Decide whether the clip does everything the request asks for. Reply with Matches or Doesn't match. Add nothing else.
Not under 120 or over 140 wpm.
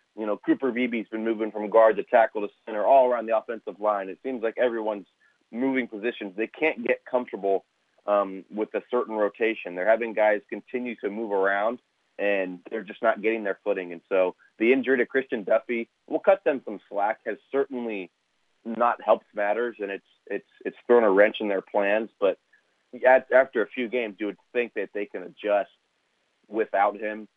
Doesn't match